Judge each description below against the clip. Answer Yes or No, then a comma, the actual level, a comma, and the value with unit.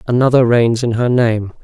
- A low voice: Yes, low, 120 Hz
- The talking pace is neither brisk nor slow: Yes, average, 185 wpm